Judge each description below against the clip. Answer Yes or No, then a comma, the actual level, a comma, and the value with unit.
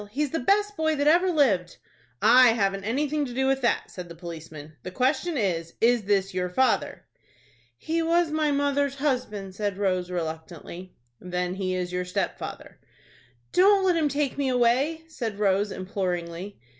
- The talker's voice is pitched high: Yes, high, 225 Hz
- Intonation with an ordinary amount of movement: No, wide, 8.0 semitones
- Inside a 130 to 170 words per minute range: Yes, average, 160 wpm